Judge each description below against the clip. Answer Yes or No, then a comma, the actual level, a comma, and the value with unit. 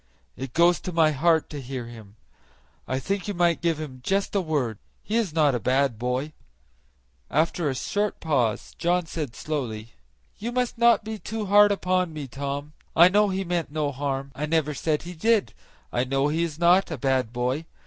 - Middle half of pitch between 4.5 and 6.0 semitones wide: Yes, average, 5.1 semitones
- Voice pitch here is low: No, medium, 155 Hz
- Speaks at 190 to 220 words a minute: Yes, average, 195 wpm